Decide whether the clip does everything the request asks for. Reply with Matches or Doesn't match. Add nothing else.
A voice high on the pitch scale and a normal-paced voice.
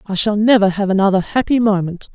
Matches